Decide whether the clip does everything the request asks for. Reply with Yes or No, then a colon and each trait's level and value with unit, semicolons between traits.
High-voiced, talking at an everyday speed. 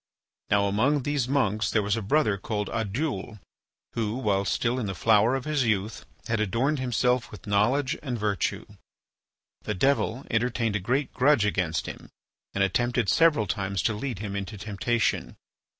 No: low, 110 Hz; average, 165 wpm